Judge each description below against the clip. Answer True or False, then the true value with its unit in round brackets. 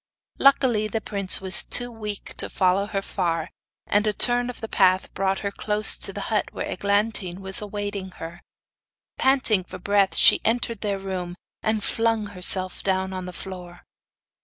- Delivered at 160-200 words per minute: True (170 wpm)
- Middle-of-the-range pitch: False (200 Hz)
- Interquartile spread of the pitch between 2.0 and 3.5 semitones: True (2.4 semitones)